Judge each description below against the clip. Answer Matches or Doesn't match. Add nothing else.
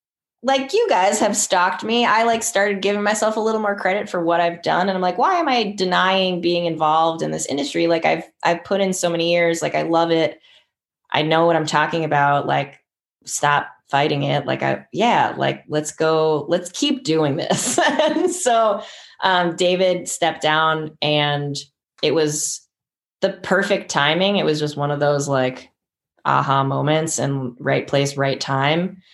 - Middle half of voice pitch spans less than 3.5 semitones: Doesn't match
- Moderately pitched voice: Matches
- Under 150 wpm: Doesn't match